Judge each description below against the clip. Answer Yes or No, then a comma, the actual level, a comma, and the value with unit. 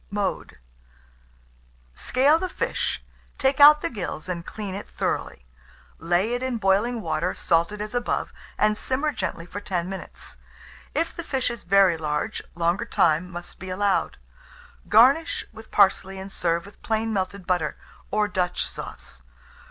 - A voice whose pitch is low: No, high, 200 Hz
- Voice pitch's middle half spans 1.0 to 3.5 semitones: No, average, 4.8 semitones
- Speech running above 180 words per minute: No, average, 150 wpm